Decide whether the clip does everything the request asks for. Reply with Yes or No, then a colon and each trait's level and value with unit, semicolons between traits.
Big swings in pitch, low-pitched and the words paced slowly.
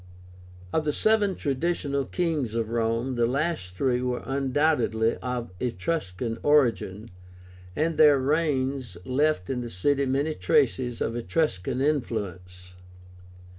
No: average, 4.6 semitones; low, 130 Hz; slow, 120 wpm